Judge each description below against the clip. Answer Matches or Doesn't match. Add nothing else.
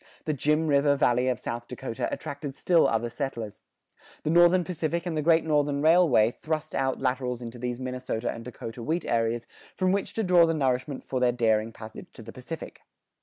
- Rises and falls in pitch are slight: Doesn't match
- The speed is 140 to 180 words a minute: Doesn't match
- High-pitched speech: Doesn't match